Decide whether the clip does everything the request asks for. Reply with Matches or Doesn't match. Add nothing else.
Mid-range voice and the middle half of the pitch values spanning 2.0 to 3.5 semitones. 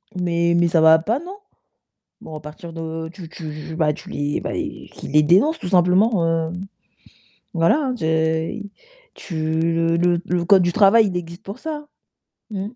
Matches